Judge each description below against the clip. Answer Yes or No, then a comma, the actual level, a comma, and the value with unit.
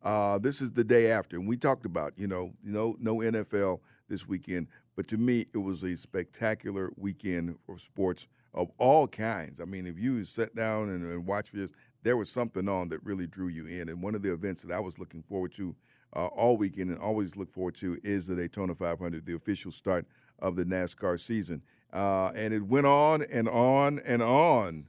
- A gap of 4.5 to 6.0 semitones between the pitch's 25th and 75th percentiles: No, average, 3.8 semitones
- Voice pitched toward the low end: Yes, very low, 95 Hz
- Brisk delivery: Yes, fast, 210 wpm